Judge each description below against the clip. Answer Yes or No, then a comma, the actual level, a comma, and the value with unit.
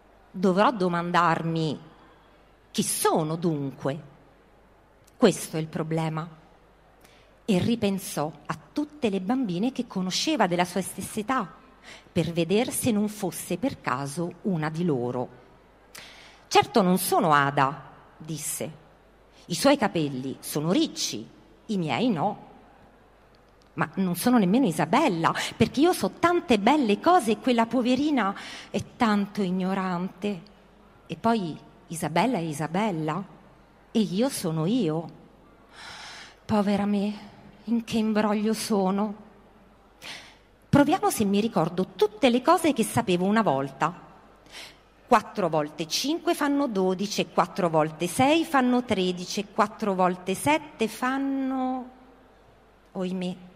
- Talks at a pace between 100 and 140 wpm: Yes, slow, 115 wpm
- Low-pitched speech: No, high, 200 Hz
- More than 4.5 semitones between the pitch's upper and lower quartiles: Yes, wide, 5.6 semitones